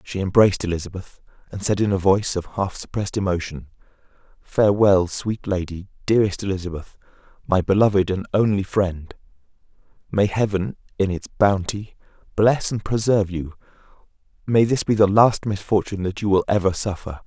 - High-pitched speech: No, low, 100 Hz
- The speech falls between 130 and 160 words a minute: Yes, average, 145 wpm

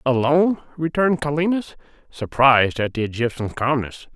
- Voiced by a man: Yes, male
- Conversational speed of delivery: No, slow, 115 wpm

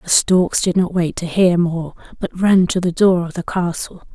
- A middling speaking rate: No, fast, 230 wpm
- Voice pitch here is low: No, medium, 175 Hz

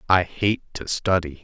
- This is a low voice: Yes, very low, 90 Hz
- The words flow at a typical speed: Yes, average, 165 wpm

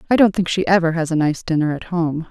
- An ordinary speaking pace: No, fast, 285 wpm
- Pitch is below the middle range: No, medium, 170 Hz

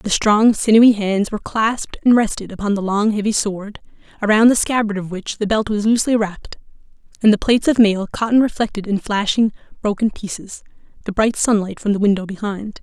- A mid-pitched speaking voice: No, high, 210 Hz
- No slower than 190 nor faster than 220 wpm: Yes, average, 195 wpm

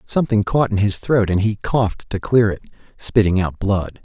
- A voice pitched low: Yes, low, 105 Hz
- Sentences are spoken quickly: Yes, fast, 210 wpm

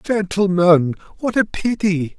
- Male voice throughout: Yes, male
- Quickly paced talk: No, slow, 110 wpm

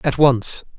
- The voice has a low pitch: Yes, low, 130 Hz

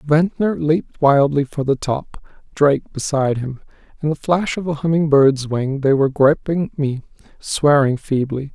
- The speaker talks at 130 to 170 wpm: Yes, average, 160 wpm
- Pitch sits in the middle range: Yes, medium, 145 Hz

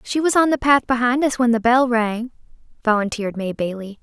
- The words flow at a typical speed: No, fast, 210 wpm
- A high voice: Yes, high, 240 Hz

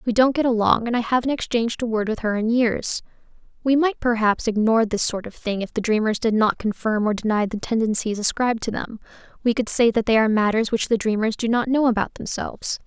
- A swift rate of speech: Yes, fast, 235 wpm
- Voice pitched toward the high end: Yes, high, 225 Hz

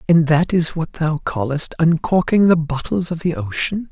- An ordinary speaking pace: Yes, average, 185 wpm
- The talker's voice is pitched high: No, medium, 160 Hz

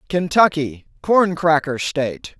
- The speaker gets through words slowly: Yes, slow, 100 wpm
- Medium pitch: Yes, medium, 160 Hz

